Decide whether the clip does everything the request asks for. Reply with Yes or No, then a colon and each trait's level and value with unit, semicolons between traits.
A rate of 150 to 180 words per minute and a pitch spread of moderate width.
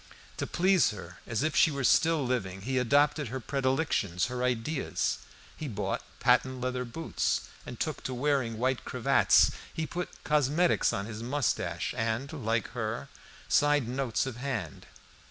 Yes: average, 155 wpm; average, 4.4 semitones